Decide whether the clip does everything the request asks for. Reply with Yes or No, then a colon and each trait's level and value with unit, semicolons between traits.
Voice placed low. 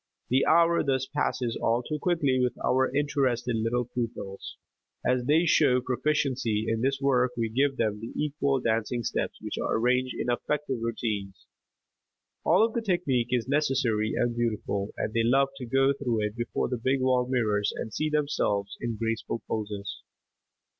Yes: low, 125 Hz